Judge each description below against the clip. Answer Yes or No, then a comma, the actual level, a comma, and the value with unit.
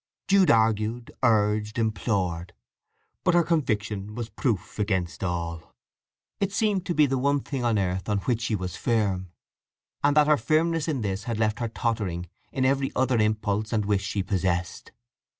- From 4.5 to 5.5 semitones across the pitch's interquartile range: Yes, average, 5.1 semitones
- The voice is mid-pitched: No, low, 110 Hz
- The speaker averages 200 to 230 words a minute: No, average, 170 wpm